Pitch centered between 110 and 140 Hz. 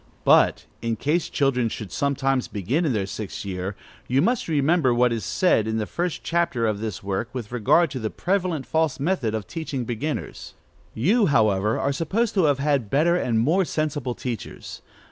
Yes: low, 135 Hz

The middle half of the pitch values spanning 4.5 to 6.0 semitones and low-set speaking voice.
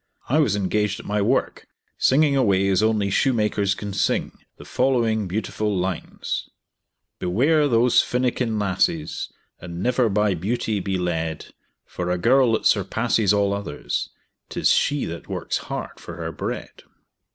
No: average, 4.1 semitones; low, 105 Hz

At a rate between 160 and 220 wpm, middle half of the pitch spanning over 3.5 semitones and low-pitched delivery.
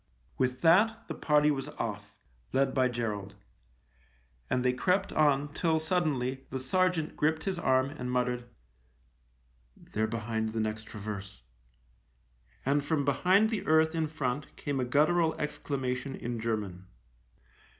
No: average, 140 wpm; wide, 5.6 semitones; low, 130 Hz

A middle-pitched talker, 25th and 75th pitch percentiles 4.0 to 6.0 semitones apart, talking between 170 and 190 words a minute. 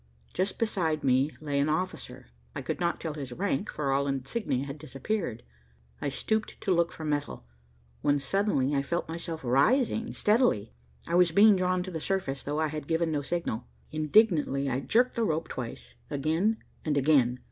Yes: medium, 155 Hz; average, 5.1 semitones; average, 180 wpm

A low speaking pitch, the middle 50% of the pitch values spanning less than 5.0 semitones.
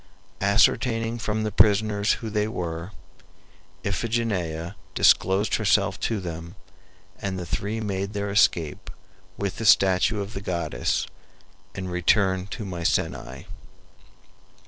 Yes: low, 100 Hz; average, 2.8 semitones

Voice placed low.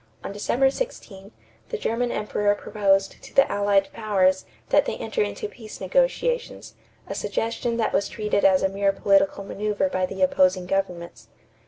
No: high, 200 Hz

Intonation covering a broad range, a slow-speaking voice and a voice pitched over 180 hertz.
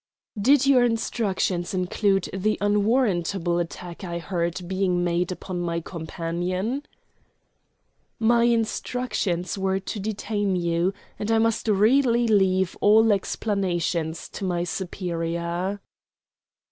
No: average, 3.8 semitones; slow, 110 wpm; high, 190 Hz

